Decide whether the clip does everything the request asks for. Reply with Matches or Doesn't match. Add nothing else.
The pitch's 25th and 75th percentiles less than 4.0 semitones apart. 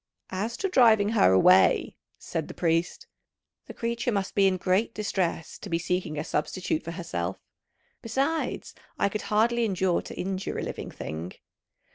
Doesn't match